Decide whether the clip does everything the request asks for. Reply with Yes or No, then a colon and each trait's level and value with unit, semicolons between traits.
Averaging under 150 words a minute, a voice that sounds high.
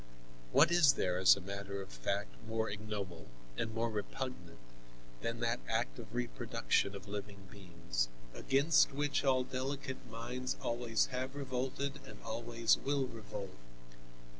No: average, 140 wpm; low, 115 Hz